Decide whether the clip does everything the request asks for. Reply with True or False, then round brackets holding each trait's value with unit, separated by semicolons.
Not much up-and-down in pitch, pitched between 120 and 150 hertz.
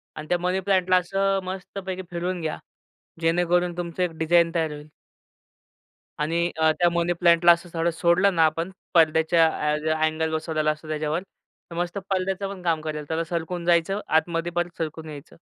False (1.9 semitones; 170 Hz)